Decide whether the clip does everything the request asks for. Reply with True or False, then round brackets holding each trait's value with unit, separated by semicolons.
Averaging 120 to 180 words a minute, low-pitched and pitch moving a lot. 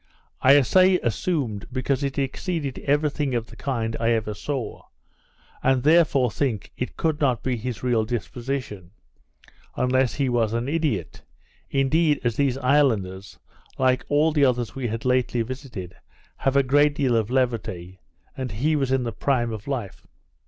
False (160 wpm; 130 Hz; 3.4 semitones)